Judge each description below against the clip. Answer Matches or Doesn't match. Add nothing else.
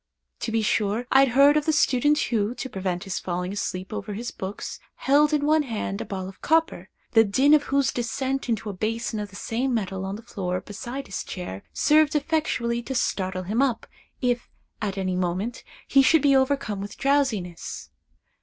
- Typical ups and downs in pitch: Doesn't match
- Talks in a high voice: Matches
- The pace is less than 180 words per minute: Doesn't match